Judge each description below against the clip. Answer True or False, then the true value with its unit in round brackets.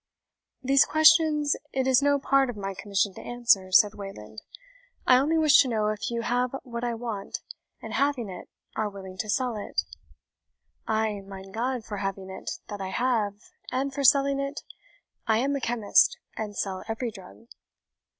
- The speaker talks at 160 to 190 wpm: True (175 wpm)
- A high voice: True (230 Hz)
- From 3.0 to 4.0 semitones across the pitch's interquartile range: False (4.9 semitones)